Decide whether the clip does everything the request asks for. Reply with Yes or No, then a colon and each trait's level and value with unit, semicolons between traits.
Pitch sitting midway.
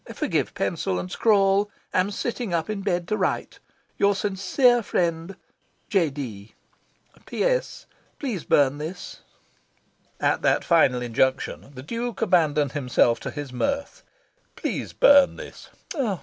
Yes: medium, 180 Hz